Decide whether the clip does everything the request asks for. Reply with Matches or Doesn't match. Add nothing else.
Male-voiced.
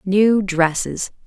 Doesn't match